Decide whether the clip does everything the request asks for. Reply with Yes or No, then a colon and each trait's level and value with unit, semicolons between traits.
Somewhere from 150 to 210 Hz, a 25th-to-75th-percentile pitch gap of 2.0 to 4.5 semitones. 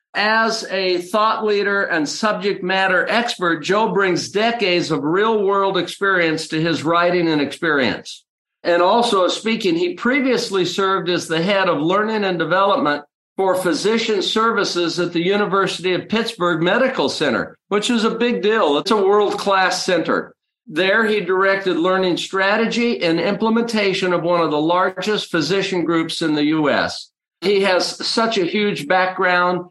Yes: high, 190 Hz; average, 3.4 semitones